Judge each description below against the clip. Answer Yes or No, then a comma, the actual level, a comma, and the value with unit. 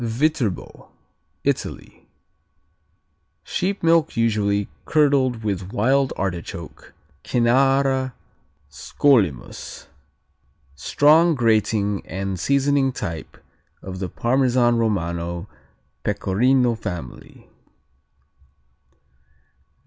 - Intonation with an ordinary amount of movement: No, wide, 6.0 semitones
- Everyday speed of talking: No, slow, 65 wpm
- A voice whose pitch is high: No, low, 115 Hz